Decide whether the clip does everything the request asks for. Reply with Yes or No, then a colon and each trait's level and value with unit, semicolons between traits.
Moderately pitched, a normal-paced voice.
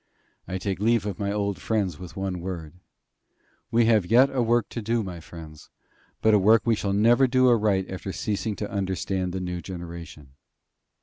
No: low, 100 Hz; average, 185 wpm